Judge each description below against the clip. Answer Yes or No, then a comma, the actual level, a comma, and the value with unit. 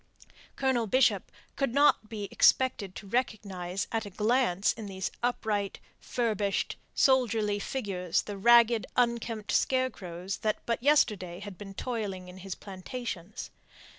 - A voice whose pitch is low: No, high, 210 Hz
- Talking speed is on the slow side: Yes, slow, 130 wpm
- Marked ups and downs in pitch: No, average, 3.7 semitones